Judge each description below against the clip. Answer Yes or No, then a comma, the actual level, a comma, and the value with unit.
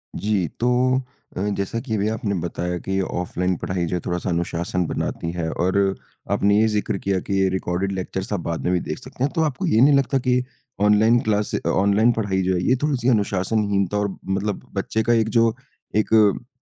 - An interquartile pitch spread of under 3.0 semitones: No, average, 3.3 semitones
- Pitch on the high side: No, low, 100 Hz